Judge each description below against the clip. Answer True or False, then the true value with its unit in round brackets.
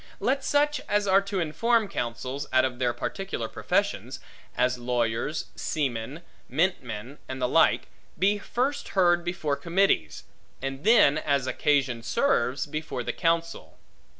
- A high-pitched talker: False (150 Hz)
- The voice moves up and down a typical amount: False (7.4 semitones)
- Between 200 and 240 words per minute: False (135 wpm)